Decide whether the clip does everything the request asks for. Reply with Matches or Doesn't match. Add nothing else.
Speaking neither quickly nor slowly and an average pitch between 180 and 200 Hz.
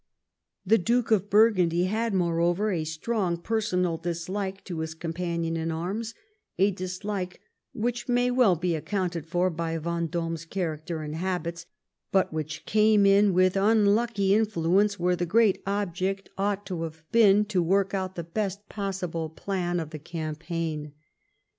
Matches